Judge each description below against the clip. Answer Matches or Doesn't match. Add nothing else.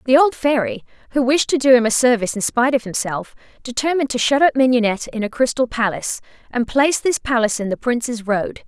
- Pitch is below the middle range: Doesn't match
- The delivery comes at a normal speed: Doesn't match